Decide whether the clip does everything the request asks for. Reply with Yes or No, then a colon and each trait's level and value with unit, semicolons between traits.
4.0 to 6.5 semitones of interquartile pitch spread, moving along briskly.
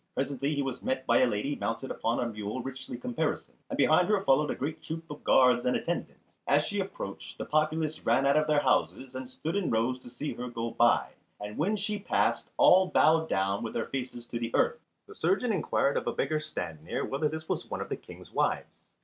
Yes: average, 4.8 semitones; fast, 225 wpm